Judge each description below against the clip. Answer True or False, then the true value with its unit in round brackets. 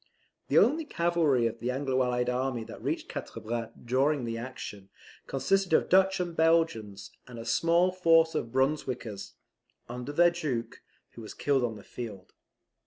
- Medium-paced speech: True (165 wpm)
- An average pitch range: False (6.0 semitones)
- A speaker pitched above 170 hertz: False (130 Hz)